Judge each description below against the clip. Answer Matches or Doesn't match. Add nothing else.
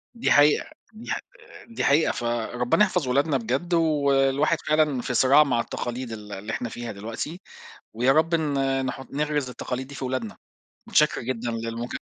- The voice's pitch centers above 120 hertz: Matches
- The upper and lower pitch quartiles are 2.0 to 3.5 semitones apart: Doesn't match